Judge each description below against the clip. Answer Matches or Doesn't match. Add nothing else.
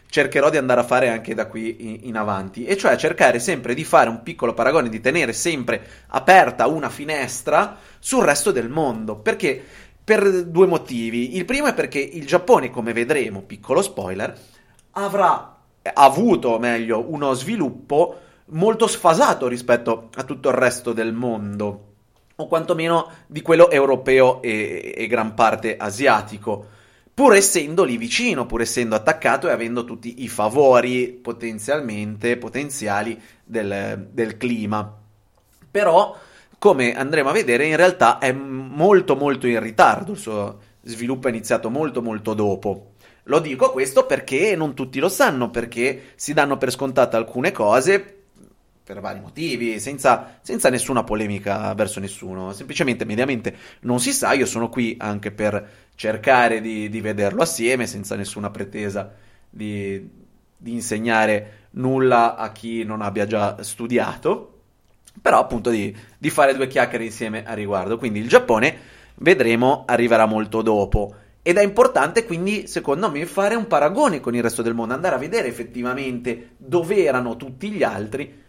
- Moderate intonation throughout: Matches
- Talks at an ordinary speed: Matches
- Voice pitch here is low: Matches